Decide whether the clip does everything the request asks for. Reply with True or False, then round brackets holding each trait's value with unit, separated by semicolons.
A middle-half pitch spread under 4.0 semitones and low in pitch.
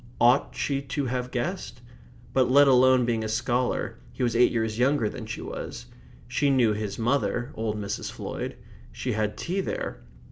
True (3.0 semitones; 125 Hz)